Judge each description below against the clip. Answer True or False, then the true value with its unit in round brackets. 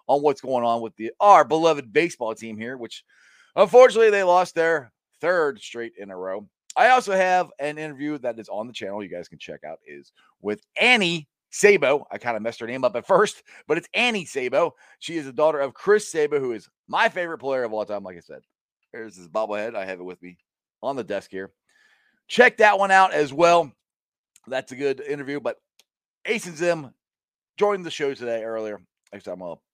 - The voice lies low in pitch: False (155 Hz)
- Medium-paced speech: False (210 wpm)